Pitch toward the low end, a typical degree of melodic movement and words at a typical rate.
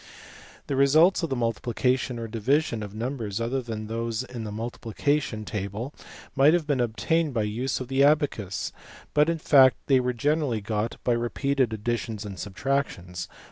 Yes: low, 120 Hz; average, 4.1 semitones; average, 175 wpm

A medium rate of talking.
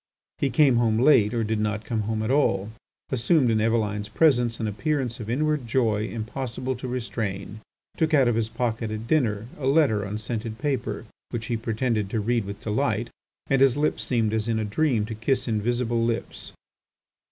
Yes: average, 185 wpm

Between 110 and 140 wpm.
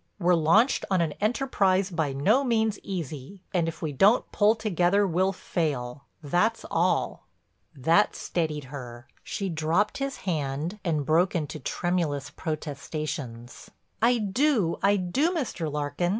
Yes: slow, 135 wpm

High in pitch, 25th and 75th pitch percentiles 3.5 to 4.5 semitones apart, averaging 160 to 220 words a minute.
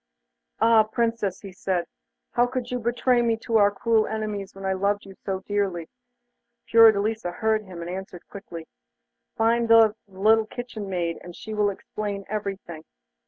No: high, 205 Hz; average, 2.8 semitones; average, 165 wpm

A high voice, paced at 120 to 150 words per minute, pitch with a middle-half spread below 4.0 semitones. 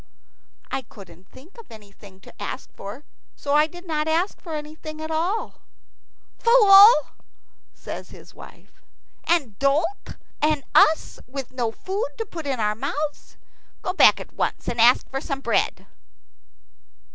No: very high, 300 Hz; average, 145 wpm; wide, 5.4 semitones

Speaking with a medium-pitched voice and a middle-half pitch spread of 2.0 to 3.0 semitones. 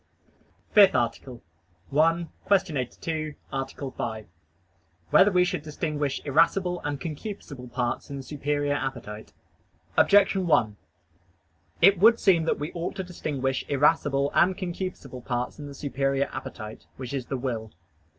No: medium, 145 Hz; average, 4.7 semitones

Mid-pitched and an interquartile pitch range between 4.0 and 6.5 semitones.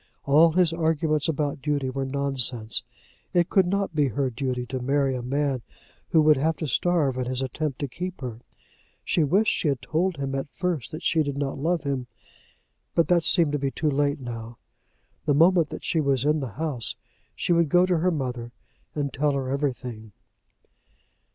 No: medium, 145 Hz; average, 3.6 semitones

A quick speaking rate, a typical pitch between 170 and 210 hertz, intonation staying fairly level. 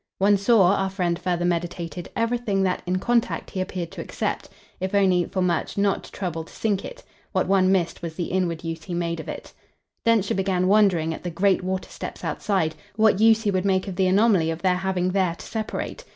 Yes: fast, 215 wpm; medium, 185 Hz; narrow, 2.3 semitones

